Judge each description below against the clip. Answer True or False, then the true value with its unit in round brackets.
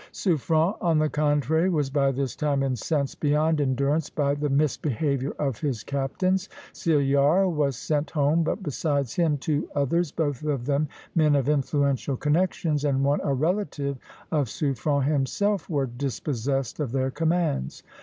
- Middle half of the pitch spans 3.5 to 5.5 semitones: False (2.4 semitones)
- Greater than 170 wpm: False (150 wpm)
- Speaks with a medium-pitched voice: True (145 Hz)